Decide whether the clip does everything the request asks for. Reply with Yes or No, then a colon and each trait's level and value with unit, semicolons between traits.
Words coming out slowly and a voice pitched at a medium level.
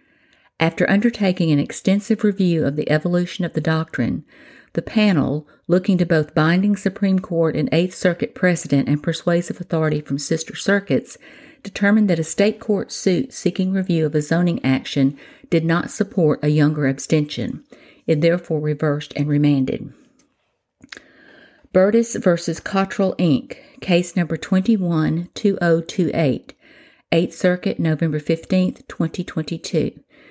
Yes: slow, 125 wpm; medium, 175 Hz